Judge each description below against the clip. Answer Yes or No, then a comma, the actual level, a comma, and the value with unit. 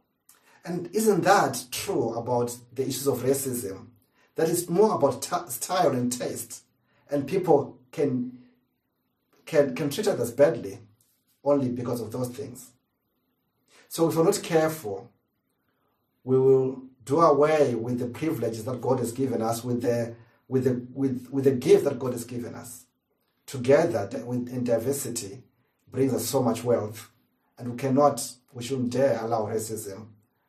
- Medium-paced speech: Yes, average, 150 wpm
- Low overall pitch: Yes, low, 125 Hz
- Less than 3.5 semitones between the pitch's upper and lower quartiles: Yes, average, 2.7 semitones